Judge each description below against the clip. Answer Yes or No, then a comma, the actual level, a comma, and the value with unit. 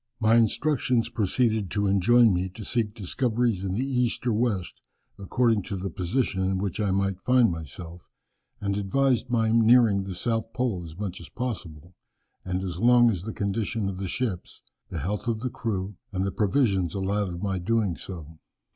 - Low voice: Yes, low, 105 Hz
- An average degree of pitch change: Yes, average, 3.7 semitones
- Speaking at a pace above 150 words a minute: Yes, average, 180 wpm